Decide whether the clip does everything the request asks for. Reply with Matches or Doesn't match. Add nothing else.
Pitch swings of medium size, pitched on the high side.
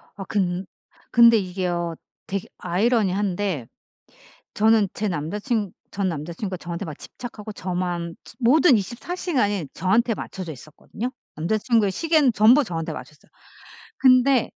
Matches